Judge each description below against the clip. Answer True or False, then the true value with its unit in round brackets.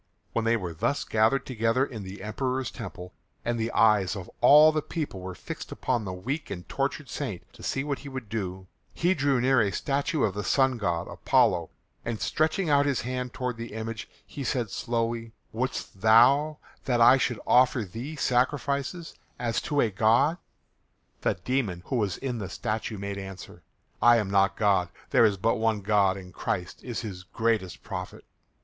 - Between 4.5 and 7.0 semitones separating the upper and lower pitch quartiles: True (4.9 semitones)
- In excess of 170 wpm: True (185 wpm)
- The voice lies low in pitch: True (115 Hz)